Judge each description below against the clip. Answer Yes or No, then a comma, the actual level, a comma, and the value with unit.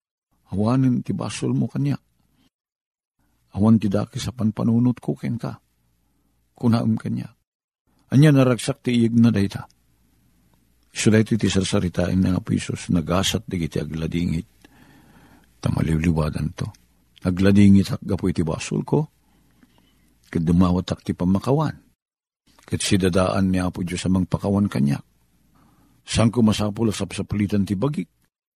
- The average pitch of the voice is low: Yes, very low, 95 Hz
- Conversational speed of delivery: Yes, average, 120 wpm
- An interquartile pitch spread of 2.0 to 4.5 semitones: No, average, 5.2 semitones